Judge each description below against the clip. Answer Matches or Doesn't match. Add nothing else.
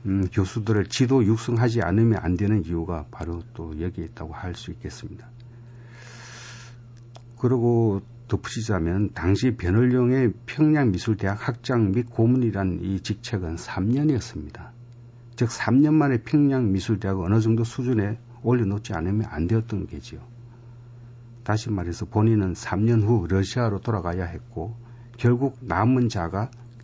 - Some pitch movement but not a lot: Matches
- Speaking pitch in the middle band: Doesn't match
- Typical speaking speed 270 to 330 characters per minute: Matches